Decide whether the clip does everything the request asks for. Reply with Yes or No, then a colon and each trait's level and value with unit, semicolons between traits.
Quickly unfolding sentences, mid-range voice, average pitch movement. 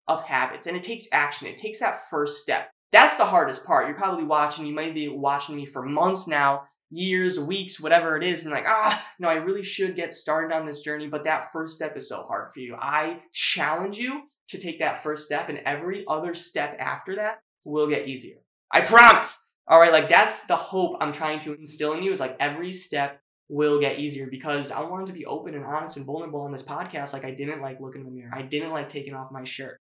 Yes: fast, 235 wpm; medium, 155 Hz; average, 3.8 semitones